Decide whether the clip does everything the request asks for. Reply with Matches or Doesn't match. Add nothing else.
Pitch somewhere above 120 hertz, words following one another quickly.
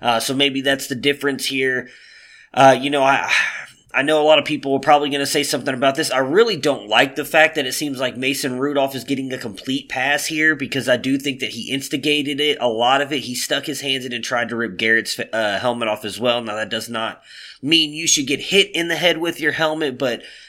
Matches